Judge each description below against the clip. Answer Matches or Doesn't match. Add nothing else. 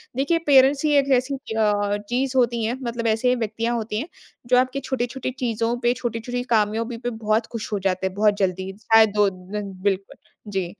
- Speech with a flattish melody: Doesn't match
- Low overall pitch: Doesn't match